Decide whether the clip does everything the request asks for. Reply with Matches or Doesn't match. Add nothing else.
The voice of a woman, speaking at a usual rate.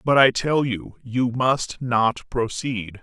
Matches